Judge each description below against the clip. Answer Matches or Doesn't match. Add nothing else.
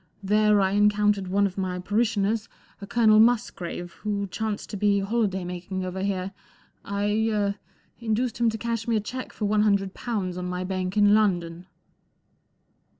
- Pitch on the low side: Doesn't match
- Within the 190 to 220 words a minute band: Doesn't match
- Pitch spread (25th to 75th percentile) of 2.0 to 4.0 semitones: Matches